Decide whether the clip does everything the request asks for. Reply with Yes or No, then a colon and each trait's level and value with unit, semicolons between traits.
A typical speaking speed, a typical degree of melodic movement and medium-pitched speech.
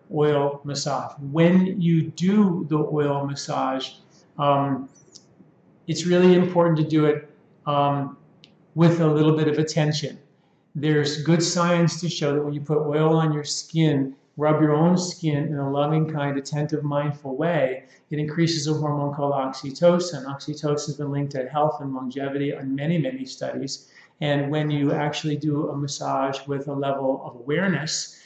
No: average, 160 wpm; narrow, 2.3 semitones; medium, 150 Hz